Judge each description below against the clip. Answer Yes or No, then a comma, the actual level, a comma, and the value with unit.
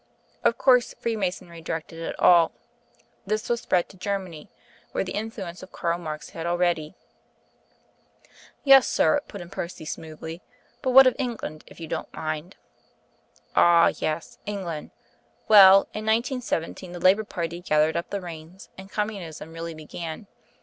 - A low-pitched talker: No, medium, 175 Hz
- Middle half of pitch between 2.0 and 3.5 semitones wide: No, average, 4.1 semitones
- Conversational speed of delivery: Yes, average, 150 wpm